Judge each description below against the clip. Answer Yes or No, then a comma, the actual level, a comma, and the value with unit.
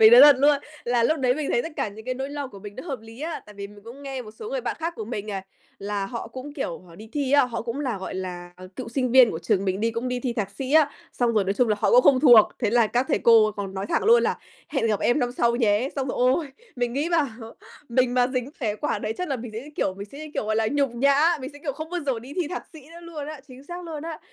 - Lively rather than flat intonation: No, average, 4.8 semitones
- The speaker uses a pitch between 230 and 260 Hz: Yes, very high, 250 Hz